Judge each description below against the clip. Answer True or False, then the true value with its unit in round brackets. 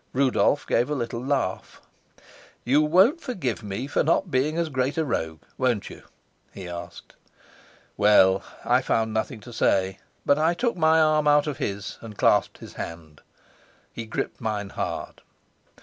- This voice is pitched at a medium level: False (125 Hz)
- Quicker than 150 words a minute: True (160 wpm)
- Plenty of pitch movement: True (6.8 semitones)